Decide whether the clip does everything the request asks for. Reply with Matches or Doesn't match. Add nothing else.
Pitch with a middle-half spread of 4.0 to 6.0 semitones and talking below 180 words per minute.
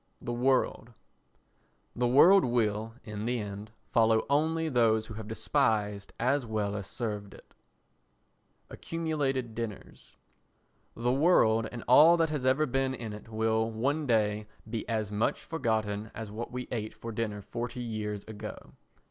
Doesn't match